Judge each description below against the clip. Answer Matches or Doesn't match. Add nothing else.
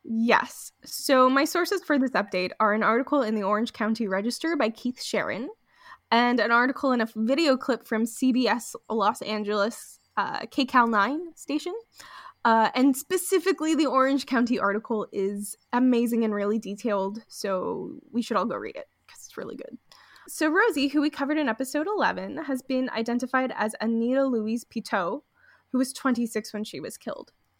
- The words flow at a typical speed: Matches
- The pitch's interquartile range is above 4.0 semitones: Matches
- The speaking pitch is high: Matches